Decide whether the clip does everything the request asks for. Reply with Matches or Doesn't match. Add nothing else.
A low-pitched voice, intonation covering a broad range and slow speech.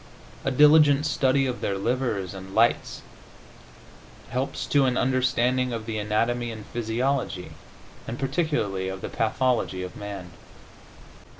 Doesn't match